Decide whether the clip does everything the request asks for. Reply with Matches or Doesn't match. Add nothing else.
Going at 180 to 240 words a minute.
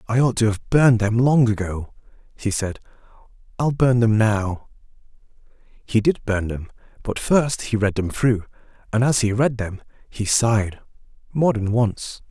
Doesn't match